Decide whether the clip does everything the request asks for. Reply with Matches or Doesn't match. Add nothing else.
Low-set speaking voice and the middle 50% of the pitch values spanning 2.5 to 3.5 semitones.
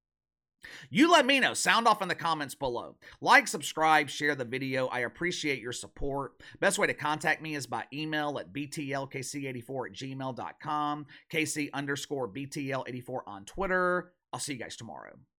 Doesn't match